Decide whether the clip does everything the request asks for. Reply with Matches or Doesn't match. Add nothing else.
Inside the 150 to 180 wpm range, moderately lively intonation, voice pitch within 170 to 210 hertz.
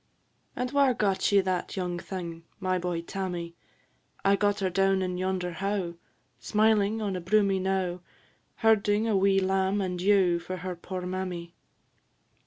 Doesn't match